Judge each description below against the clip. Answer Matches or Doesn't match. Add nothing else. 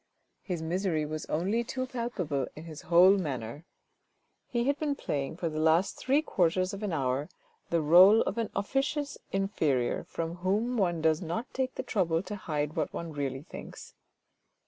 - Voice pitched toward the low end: Doesn't match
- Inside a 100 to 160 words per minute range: Doesn't match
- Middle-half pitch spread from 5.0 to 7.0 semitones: Matches